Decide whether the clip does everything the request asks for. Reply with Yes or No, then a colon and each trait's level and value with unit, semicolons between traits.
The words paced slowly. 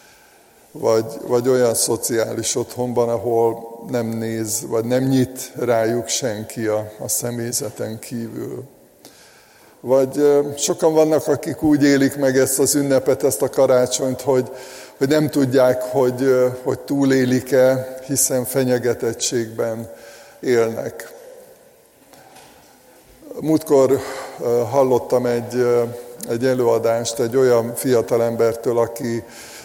Yes: slow, 100 wpm